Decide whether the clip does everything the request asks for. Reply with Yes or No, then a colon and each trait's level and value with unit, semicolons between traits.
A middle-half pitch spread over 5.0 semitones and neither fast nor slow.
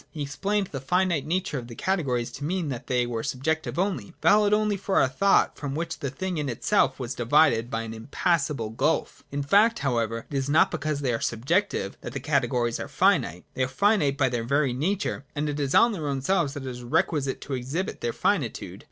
No: wide, 5.4 semitones; fast, 220 wpm